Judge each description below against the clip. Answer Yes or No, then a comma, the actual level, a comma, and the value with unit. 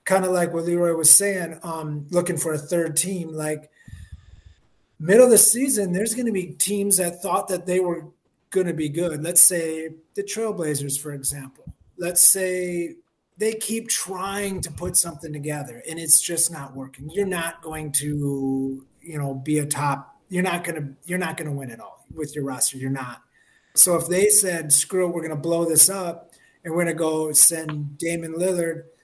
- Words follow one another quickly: No, average, 190 wpm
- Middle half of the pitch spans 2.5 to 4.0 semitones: Yes, average, 3.3 semitones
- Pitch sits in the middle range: Yes, medium, 165 Hz